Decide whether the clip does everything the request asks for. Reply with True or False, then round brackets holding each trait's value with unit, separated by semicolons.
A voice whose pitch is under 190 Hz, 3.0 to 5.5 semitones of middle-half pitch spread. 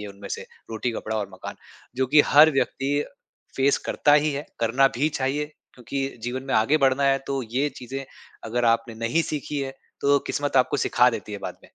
True (135 Hz; 3.6 semitones)